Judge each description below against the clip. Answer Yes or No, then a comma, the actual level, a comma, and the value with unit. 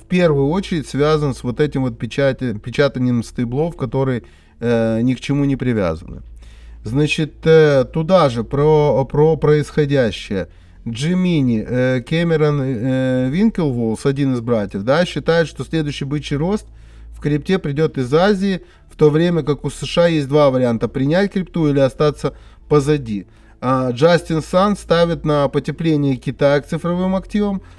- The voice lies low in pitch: No, medium, 145 Hz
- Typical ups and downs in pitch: Yes, average, 4.2 semitones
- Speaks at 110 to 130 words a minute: No, average, 145 wpm